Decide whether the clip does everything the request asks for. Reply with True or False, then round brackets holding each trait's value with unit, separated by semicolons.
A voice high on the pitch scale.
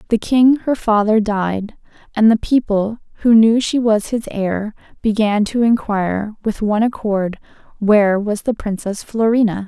True (215 Hz)